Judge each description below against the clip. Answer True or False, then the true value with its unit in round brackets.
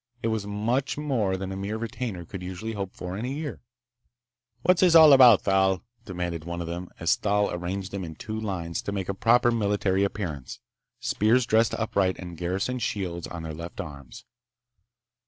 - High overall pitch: False (100 Hz)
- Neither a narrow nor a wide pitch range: True (4.3 semitones)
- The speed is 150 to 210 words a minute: True (185 wpm)